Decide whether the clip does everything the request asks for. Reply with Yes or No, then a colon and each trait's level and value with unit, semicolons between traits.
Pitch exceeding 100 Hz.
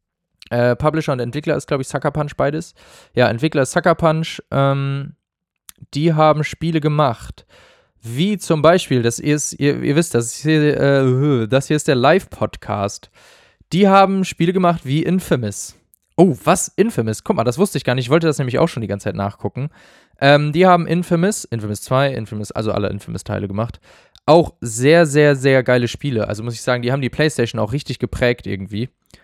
Yes: medium, 140 Hz